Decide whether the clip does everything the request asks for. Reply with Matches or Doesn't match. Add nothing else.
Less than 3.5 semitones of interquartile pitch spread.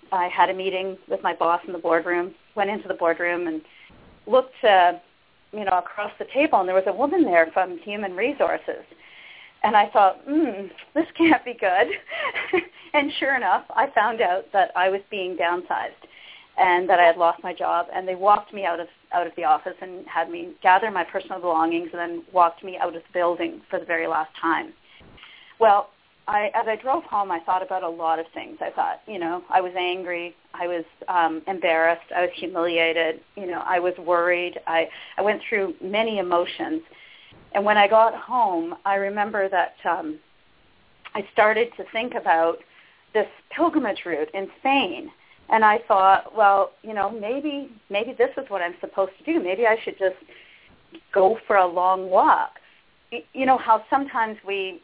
Doesn't match